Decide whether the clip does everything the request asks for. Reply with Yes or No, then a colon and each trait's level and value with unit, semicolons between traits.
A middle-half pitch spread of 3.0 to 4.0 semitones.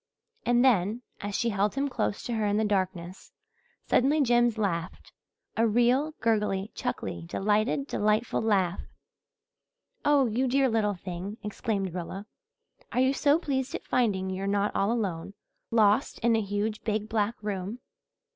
Yes: average, 3.4 semitones